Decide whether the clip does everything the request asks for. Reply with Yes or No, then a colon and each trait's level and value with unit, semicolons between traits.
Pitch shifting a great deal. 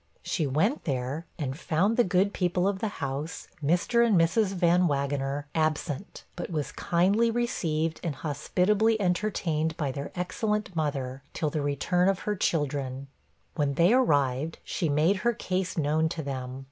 No: average, 4.8 semitones